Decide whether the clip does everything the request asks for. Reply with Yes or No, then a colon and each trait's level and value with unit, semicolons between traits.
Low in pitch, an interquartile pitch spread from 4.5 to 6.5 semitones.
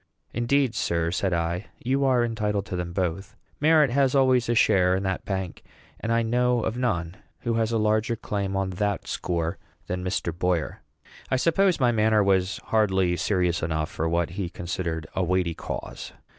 Yes: low, 100 Hz; average, 4.8 semitones